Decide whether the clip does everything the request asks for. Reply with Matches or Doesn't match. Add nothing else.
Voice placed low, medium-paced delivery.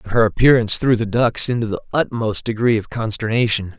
Matches